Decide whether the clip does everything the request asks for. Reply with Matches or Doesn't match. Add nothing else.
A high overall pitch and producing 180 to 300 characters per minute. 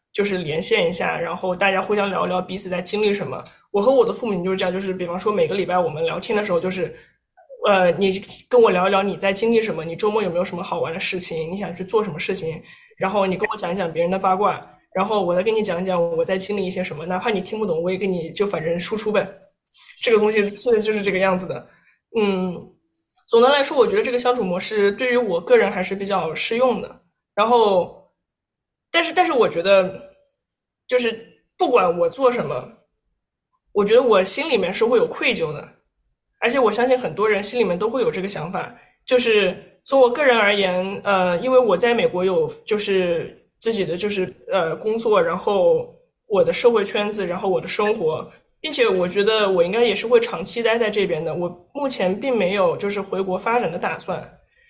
Doesn't match